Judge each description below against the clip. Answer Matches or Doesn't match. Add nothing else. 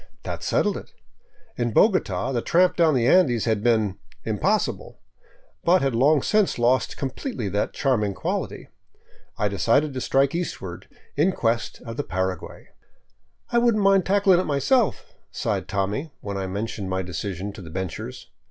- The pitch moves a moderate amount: Doesn't match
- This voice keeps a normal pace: Matches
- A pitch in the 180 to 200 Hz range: Doesn't match